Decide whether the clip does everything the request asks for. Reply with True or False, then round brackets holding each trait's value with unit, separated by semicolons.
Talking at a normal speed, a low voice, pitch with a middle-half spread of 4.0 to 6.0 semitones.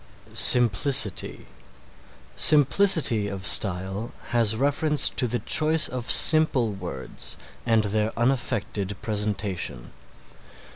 False (90 wpm; 115 Hz; 5.1 semitones)